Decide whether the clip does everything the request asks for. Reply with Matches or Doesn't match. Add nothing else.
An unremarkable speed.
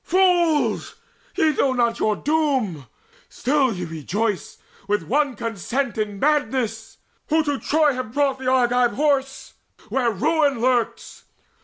Doesn't match